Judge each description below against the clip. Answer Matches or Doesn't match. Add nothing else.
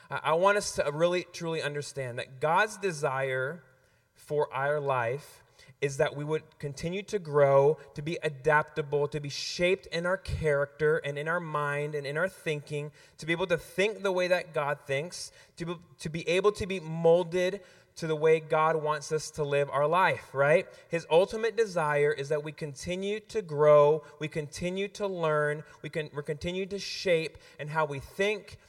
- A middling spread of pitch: Matches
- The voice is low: Doesn't match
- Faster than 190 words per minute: Doesn't match